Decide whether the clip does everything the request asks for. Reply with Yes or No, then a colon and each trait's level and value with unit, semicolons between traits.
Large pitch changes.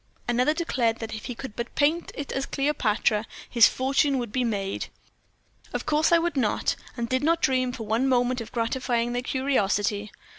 No: average, 3.2 semitones